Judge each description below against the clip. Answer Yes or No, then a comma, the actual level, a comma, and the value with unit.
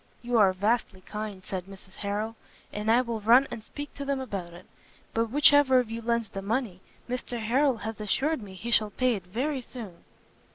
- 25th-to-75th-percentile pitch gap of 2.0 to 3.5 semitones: No, average, 3.9 semitones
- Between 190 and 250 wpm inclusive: Yes, fast, 205 wpm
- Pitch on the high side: Yes, high, 225 Hz